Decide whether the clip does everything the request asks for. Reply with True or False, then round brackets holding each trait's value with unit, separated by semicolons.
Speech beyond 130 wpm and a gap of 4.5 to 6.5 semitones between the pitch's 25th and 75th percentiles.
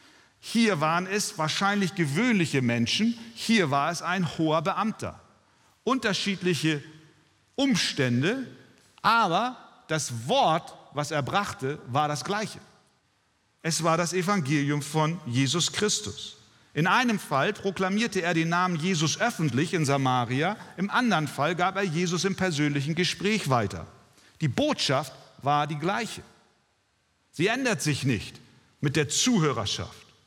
False (125 wpm; 5.3 semitones)